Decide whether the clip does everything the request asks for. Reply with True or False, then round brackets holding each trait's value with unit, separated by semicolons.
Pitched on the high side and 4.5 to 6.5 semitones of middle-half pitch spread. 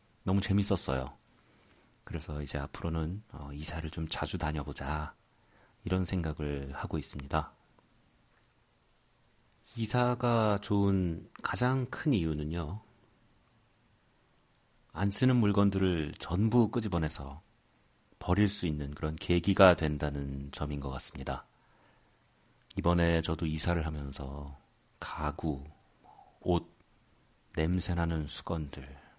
False (85 Hz; 5.5 semitones)